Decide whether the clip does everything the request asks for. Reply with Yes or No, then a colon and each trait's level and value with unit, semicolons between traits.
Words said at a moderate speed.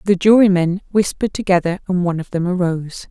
Yes: average, 175 wpm